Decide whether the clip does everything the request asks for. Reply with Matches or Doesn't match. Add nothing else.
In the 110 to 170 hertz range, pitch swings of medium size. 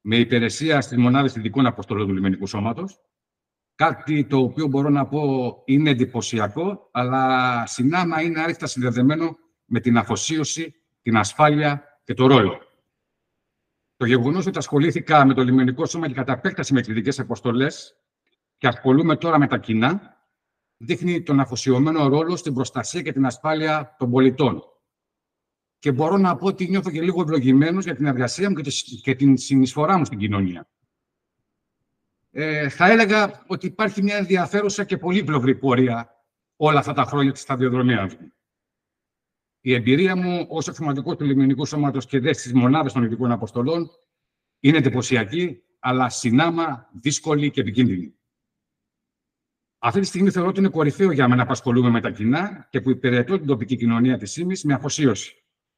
Matches